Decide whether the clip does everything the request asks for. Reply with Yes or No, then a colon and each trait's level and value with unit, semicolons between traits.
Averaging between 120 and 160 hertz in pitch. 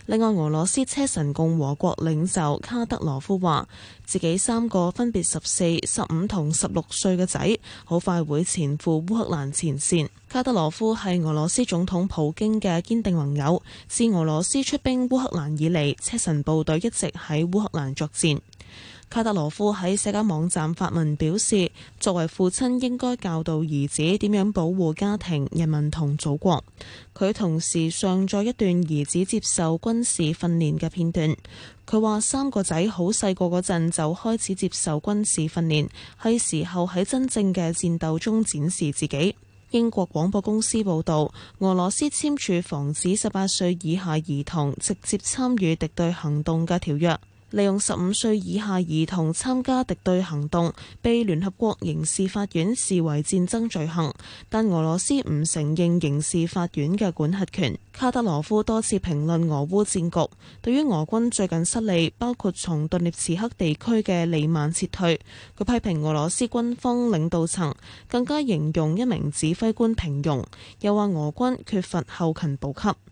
No: medium, 175 Hz